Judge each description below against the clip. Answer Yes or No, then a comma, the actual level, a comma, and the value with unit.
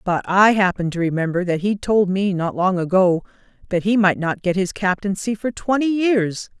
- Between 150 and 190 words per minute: No, average, 200 wpm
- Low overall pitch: No, high, 195 Hz